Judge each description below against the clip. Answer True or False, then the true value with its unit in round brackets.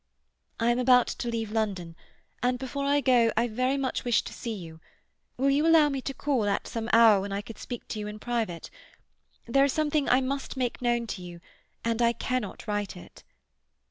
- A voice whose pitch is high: True (240 Hz)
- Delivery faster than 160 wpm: True (205 wpm)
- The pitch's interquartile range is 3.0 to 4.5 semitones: True (3.6 semitones)